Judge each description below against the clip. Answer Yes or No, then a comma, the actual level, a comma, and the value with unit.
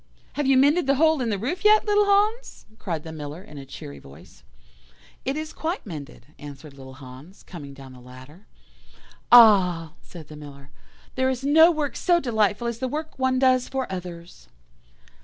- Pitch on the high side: Yes, high, 210 Hz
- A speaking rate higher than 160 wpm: Yes, average, 180 wpm